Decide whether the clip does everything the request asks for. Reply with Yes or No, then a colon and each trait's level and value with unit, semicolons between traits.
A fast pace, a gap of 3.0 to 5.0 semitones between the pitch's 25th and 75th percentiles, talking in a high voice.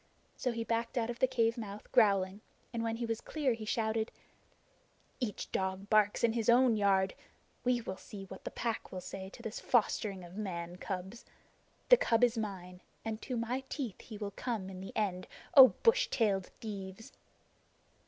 No: average, 185 wpm; average, 3.4 semitones; high, 220 Hz